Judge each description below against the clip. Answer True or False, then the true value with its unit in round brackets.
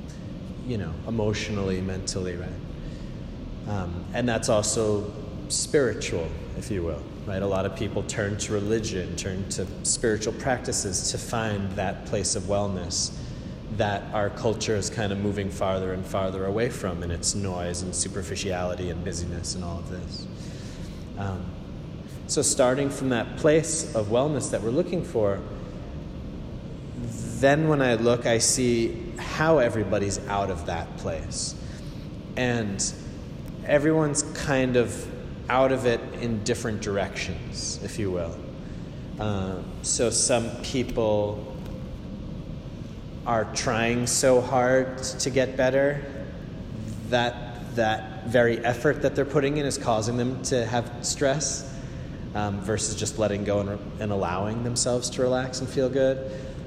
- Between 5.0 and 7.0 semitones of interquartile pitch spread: False (4.3 semitones)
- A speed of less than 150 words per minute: True (140 wpm)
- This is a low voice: True (110 Hz)